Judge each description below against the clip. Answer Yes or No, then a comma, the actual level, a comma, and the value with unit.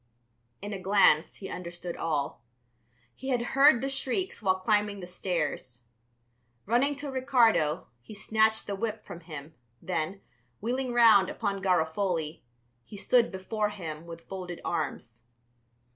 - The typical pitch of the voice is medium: No, high, 195 Hz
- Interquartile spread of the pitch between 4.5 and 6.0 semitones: Yes, wide, 5.4 semitones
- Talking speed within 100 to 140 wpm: Yes, slow, 135 wpm